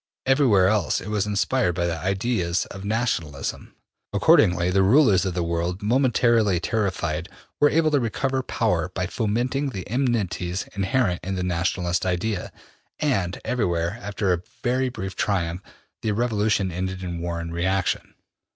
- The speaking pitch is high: No, very low, 95 Hz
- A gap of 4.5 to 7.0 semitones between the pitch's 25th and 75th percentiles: Yes, average, 4.9 semitones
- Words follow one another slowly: No, average, 150 wpm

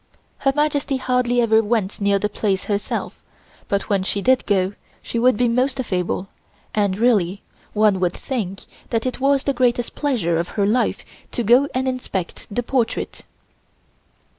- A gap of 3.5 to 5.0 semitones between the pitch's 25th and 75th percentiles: Yes, average, 4.2 semitones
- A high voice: Yes, high, 230 Hz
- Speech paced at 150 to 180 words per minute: Yes, average, 165 wpm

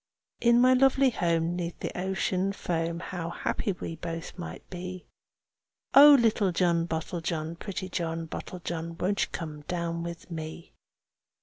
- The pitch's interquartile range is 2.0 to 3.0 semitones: Yes, narrow, 2.4 semitones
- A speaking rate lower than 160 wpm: Yes, average, 140 wpm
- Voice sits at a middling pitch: Yes, medium, 175 Hz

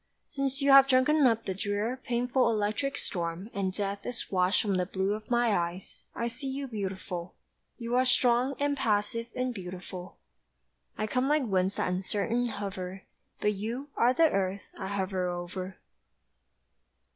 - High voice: Yes, high, 210 Hz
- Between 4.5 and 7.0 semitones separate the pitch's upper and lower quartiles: Yes, average, 4.9 semitones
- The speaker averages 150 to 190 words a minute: Yes, average, 160 wpm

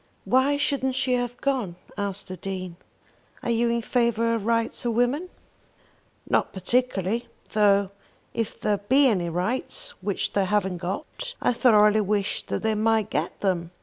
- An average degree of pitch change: Yes, average, 3.8 semitones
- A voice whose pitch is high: Yes, high, 220 Hz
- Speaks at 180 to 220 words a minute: No, average, 155 wpm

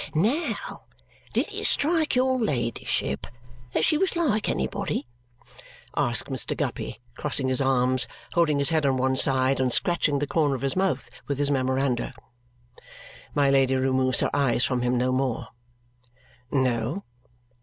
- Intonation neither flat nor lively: Yes, average, 4.6 semitones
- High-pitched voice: No, low, 135 Hz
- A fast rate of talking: No, average, 145 wpm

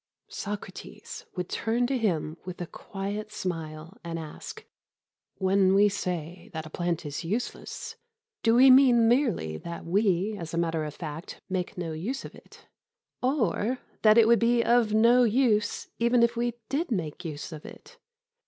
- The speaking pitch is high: Yes, high, 200 Hz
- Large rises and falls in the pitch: Yes, wide, 5.8 semitones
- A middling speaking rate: Yes, average, 165 wpm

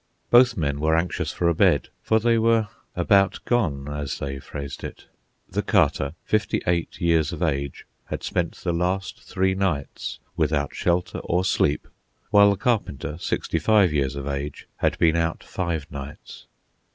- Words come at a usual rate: Yes, average, 165 wpm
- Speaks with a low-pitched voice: Yes, very low, 85 Hz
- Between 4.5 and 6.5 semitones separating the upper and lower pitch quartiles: Yes, average, 5.1 semitones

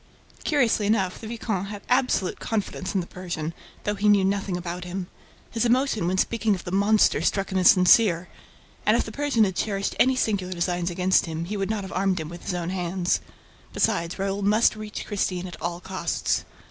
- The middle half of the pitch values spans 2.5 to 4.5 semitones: Yes, average, 3.0 semitones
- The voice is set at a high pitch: Yes, high, 195 Hz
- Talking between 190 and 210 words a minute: Yes, average, 200 wpm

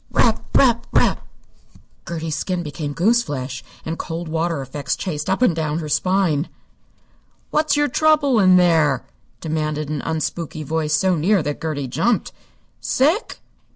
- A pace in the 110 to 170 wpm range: Yes, average, 140 wpm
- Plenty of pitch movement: No, average, 4.2 semitones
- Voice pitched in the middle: Yes, medium, 165 Hz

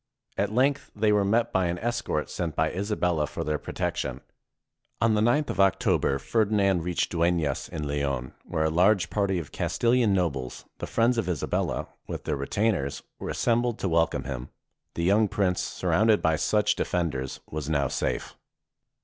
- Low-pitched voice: Yes, very low, 90 Hz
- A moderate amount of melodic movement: No, wide, 5.8 semitones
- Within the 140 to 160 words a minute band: No, average, 175 wpm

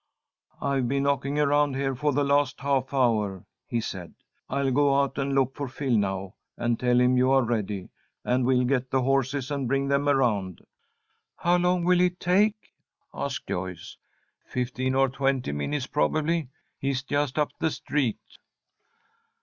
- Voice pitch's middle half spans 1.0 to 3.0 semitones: Yes, narrow, 2.5 semitones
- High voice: No, low, 135 Hz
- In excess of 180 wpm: No, average, 160 wpm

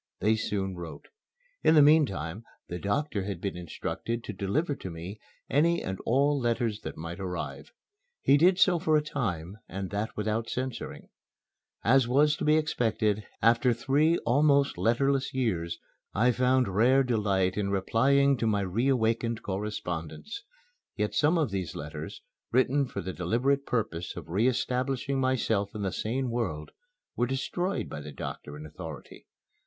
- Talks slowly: No, average, 160 wpm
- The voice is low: Yes, low, 115 Hz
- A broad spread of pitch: Yes, wide, 5.9 semitones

